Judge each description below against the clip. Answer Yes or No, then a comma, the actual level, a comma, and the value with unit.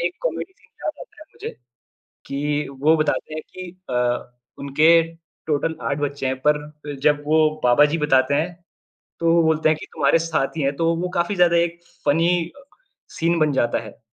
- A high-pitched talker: No, medium, 155 Hz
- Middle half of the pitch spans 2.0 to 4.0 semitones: Yes, narrow, 2.6 semitones